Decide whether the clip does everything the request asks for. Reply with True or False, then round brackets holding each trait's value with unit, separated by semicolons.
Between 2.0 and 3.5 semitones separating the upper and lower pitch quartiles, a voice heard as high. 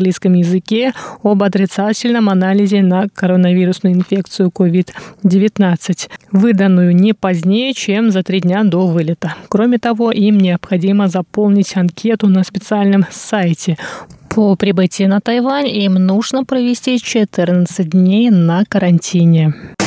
True (2.5 semitones; 195 Hz)